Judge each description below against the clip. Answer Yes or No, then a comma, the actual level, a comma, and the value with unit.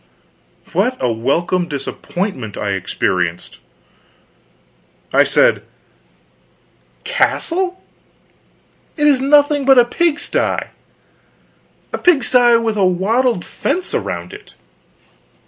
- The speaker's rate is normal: No, slow, 90 wpm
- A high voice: Yes, high, 235 Hz